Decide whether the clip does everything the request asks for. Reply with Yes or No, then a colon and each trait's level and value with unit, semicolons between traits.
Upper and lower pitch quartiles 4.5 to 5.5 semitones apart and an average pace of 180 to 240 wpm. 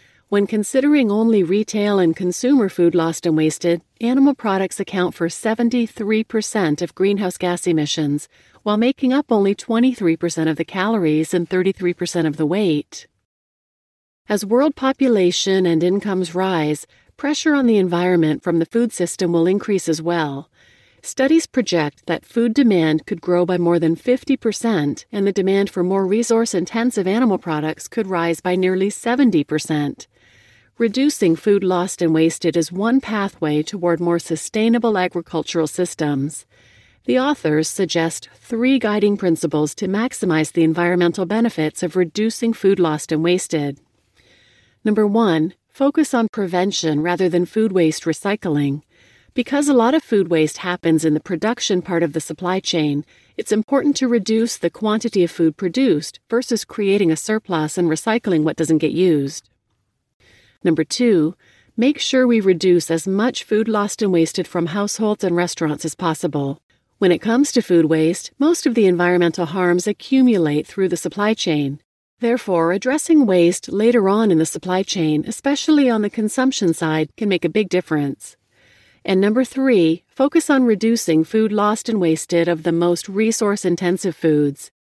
No: average, 5.2 semitones; average, 155 wpm